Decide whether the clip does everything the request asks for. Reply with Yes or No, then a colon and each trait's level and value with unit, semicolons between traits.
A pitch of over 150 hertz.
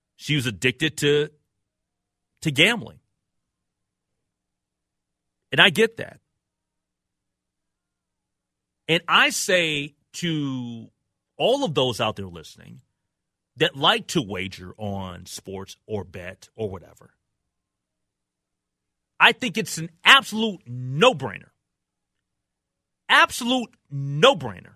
No: low, 130 Hz